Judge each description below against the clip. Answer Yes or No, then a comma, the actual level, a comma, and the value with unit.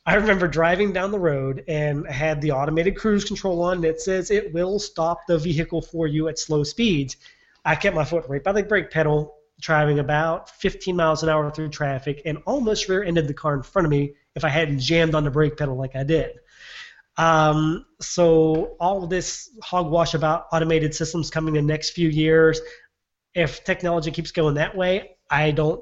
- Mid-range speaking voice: Yes, medium, 160 Hz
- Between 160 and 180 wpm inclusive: No, average, 200 wpm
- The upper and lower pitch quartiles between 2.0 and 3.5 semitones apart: Yes, average, 2.7 semitones